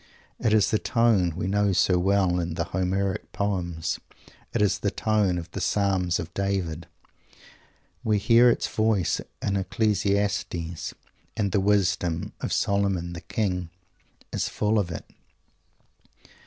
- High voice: No, low, 100 Hz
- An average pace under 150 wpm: Yes, average, 140 wpm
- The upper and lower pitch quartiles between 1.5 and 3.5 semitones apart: Yes, narrow, 2.6 semitones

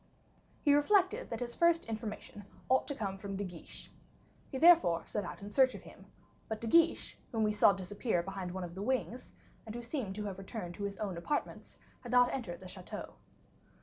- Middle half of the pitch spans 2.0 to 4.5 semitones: No, average, 5.1 semitones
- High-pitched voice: Yes, high, 215 Hz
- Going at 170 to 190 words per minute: No, fast, 205 wpm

